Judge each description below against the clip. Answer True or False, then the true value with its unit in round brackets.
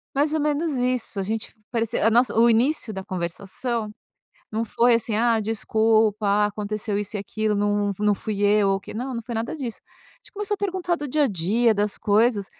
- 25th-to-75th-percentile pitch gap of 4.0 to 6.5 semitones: False (3.0 semitones)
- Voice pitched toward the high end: True (220 Hz)